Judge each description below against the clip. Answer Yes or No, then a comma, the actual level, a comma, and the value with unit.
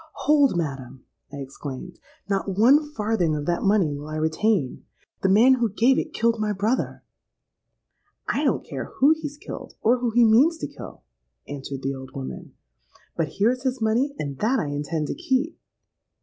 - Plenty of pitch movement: Yes, wide, 9.0 semitones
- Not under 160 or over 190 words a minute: Yes, average, 170 wpm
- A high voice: Yes, high, 210 Hz